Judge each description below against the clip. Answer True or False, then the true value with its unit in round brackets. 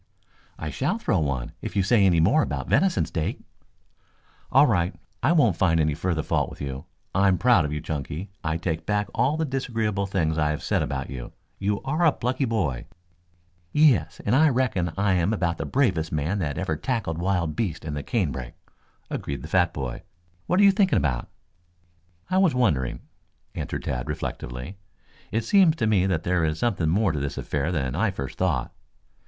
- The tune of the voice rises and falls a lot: True (6.9 semitones)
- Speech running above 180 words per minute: True (190 wpm)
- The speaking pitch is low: True (90 Hz)